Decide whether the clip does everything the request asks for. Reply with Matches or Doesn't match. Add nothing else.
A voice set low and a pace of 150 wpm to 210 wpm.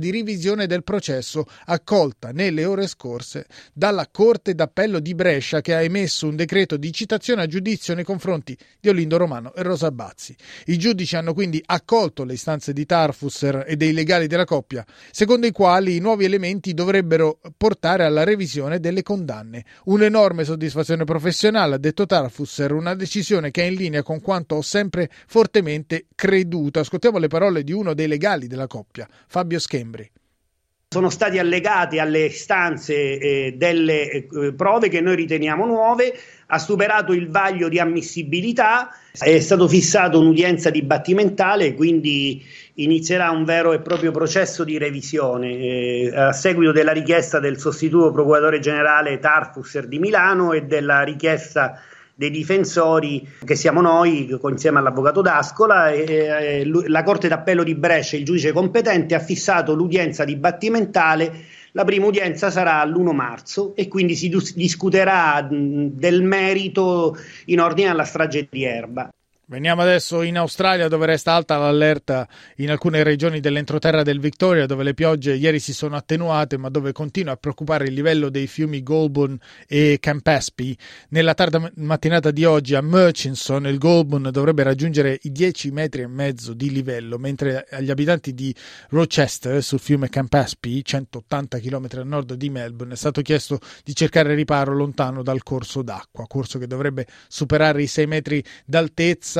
Doesn't match